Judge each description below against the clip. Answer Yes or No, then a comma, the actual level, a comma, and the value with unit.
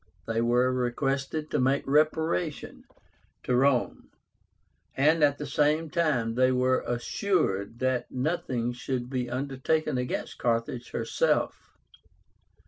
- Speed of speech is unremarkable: No, slow, 115 wpm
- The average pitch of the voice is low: Yes, low, 130 Hz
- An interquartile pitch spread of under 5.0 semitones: Yes, average, 3.5 semitones